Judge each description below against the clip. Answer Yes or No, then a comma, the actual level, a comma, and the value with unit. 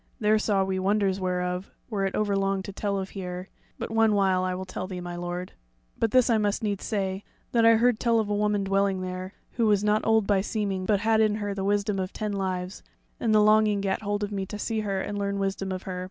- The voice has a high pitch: Yes, high, 200 Hz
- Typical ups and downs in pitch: No, narrow, 2.0 semitones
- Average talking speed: No, fast, 245 wpm